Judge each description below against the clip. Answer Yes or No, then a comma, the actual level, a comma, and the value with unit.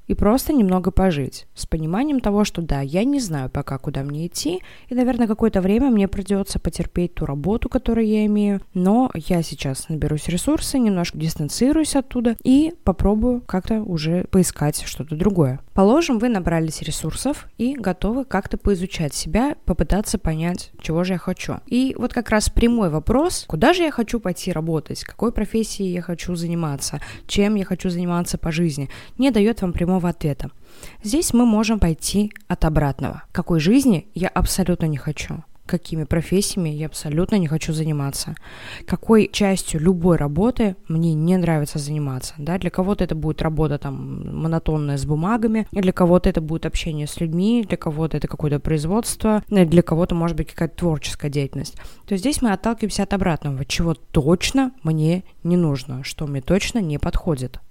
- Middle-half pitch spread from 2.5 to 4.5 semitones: No, average, 5.1 semitones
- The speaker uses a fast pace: Yes, fast, 165 wpm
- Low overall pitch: No, medium, 180 Hz